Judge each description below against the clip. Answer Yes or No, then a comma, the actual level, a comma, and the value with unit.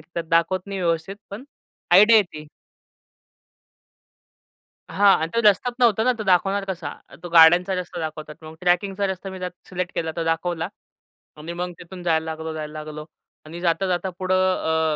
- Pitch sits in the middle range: Yes, medium, 175 Hz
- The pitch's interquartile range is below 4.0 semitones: Yes, average, 2.9 semitones